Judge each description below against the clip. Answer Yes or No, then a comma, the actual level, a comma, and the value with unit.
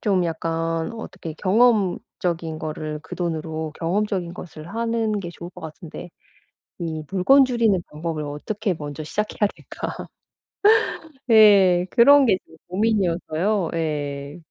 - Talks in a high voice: No, medium, 175 Hz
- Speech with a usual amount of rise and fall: Yes, average, 4.7 semitones